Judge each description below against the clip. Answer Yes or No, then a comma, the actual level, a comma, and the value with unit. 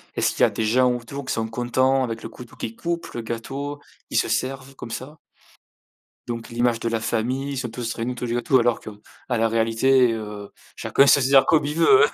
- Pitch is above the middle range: No, low, 125 Hz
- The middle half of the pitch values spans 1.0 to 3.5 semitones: Yes, average, 2.8 semitones